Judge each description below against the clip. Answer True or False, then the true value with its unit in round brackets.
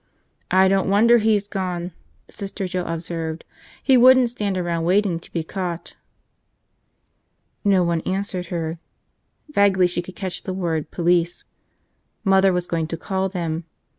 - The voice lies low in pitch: False (185 Hz)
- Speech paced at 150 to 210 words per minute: False (140 wpm)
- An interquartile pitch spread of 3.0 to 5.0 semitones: False (2.5 semitones)